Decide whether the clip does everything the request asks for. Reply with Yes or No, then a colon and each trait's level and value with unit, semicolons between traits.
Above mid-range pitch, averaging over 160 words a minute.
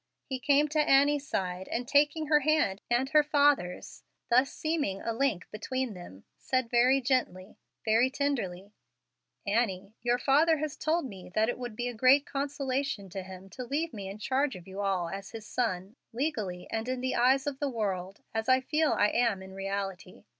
Yes: high, 245 Hz; average, 190 wpm